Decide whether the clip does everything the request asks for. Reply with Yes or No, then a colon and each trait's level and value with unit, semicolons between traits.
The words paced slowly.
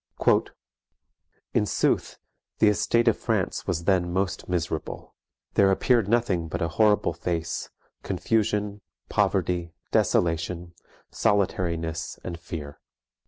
Yes: slow, 105 wpm